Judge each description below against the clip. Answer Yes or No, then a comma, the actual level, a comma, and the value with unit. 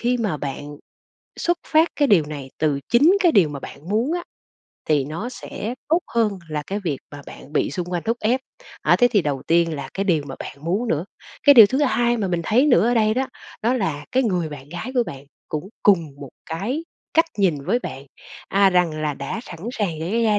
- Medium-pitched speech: No, high, 195 Hz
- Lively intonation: Yes, wide, 7.7 semitones